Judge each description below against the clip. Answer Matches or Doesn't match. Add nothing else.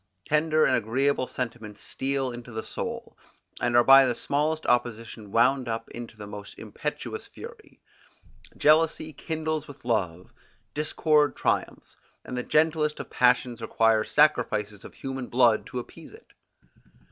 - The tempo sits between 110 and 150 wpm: Matches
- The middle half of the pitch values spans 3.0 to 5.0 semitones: Matches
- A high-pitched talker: Doesn't match